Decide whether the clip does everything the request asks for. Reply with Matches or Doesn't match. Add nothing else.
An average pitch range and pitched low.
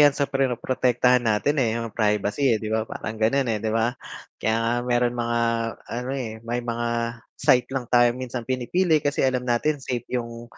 Doesn't match